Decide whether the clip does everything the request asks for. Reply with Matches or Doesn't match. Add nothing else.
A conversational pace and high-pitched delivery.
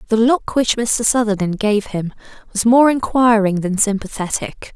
Matches